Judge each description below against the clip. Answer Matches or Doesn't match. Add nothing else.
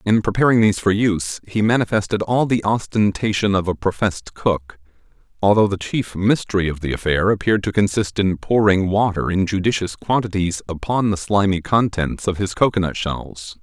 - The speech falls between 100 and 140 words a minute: Doesn't match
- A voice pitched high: Doesn't match